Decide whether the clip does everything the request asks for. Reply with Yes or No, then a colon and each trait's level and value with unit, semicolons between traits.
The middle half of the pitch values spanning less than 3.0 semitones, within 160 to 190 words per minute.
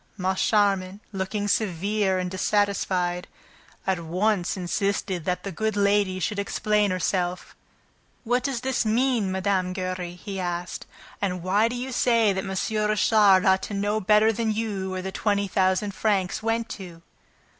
No: narrow, 2.5 semitones; average, 150 wpm